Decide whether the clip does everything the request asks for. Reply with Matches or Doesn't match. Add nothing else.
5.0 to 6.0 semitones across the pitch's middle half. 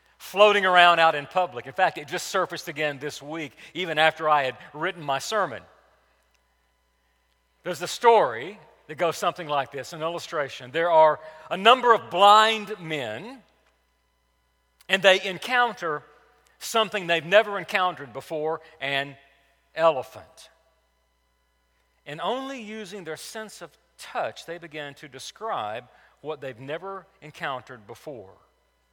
Matches